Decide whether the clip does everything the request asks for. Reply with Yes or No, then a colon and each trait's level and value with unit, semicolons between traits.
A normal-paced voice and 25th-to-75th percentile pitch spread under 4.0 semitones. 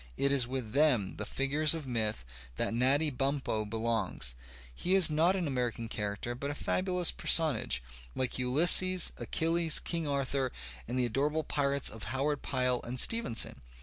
No: average, 150 wpm; average, 4.7 semitones